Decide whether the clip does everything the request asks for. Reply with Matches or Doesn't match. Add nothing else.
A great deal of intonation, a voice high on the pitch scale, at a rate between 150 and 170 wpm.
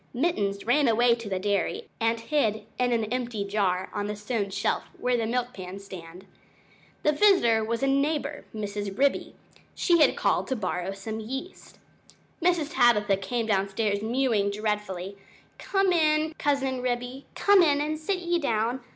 Matches